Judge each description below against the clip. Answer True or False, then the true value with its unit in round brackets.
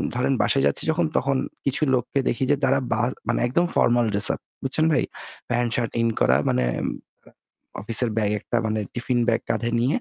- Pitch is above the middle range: False (120 Hz)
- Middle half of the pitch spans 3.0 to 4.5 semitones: False (2.6 semitones)